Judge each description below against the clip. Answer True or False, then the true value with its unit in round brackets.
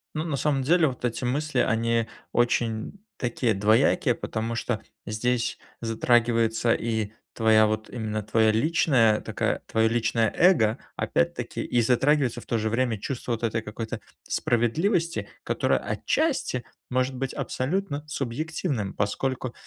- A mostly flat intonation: False (3.5 semitones)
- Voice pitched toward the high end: False (120 Hz)